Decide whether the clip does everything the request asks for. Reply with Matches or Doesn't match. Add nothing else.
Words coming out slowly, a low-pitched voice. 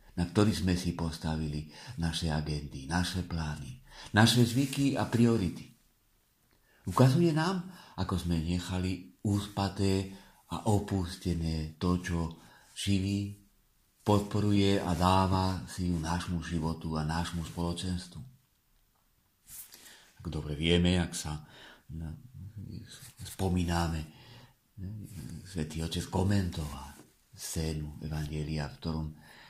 Matches